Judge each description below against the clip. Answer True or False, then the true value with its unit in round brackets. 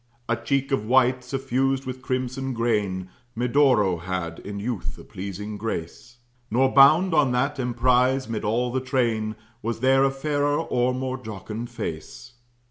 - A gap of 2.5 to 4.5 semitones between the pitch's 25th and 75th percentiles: True (3.5 semitones)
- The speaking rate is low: False (150 wpm)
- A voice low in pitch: True (125 Hz)